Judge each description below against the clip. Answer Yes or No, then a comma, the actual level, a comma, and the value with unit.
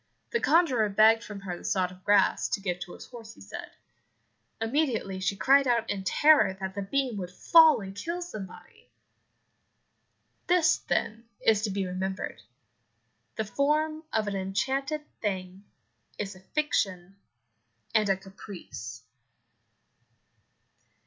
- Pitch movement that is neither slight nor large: No, wide, 5.9 semitones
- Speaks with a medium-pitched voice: No, high, 205 Hz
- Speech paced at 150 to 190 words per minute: No, slow, 135 wpm